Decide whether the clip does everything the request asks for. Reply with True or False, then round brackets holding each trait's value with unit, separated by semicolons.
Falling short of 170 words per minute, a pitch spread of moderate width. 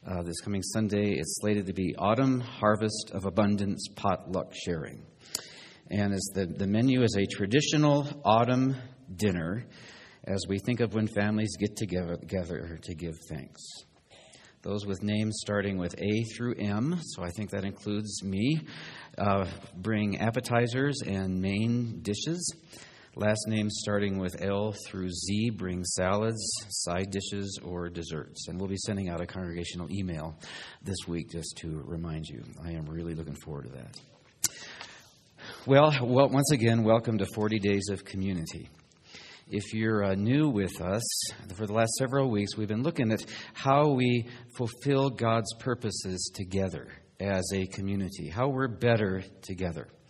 True (155 wpm; 3.3 semitones)